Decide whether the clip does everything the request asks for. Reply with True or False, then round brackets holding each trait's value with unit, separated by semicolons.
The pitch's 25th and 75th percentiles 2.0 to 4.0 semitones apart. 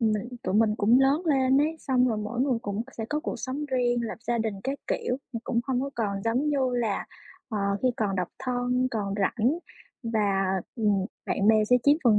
True (3.7 semitones)